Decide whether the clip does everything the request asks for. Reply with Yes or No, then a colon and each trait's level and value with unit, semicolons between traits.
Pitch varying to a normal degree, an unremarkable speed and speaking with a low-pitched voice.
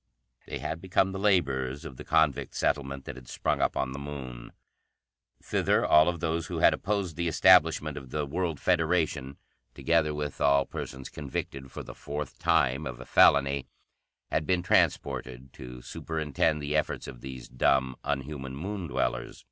Yes: average, 3.4 semitones; average, 165 wpm; very low, 70 Hz